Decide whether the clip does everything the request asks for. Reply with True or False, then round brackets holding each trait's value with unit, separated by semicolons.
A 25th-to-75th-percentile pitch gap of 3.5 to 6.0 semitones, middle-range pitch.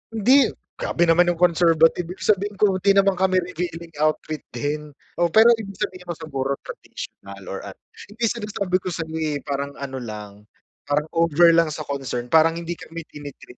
True (4.2 semitones; 165 Hz)